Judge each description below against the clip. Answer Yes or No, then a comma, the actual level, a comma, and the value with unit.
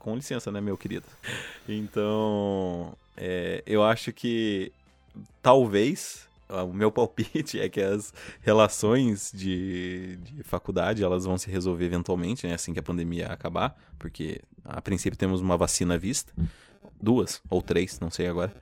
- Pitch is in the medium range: No, very low, 95 Hz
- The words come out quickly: No, average, 150 wpm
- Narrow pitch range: No, average, 3.2 semitones